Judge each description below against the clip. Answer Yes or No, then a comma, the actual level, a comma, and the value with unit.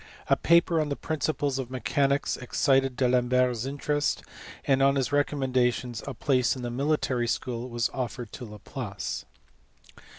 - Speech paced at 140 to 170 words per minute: Yes, average, 155 wpm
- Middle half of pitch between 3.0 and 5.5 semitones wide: No, narrow, 2.5 semitones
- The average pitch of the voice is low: Yes, low, 130 Hz